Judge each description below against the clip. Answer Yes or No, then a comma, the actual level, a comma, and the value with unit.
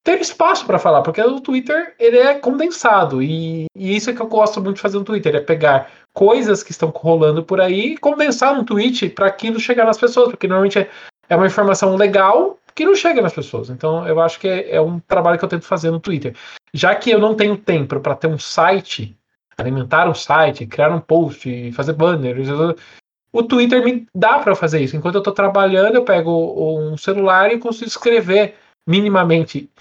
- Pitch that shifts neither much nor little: No, wide, 6.1 semitones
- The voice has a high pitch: Yes, high, 195 Hz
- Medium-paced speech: No, fast, 205 wpm